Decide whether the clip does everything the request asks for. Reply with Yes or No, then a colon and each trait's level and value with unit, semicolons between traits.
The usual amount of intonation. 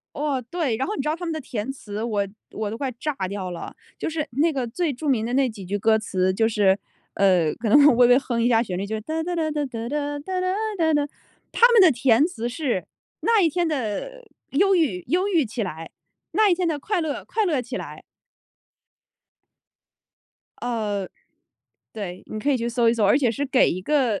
No: wide, 6.5 semitones